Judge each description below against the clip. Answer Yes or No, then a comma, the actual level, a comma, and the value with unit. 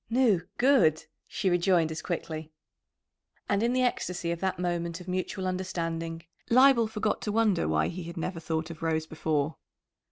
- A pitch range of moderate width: Yes, average, 4.0 semitones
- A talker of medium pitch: Yes, medium, 175 Hz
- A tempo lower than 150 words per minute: No, average, 165 wpm